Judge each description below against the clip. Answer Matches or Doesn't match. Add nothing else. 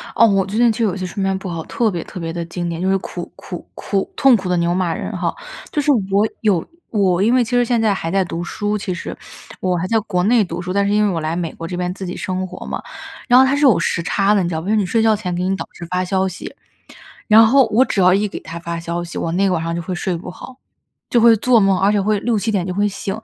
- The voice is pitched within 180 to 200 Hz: Matches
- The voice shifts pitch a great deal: Doesn't match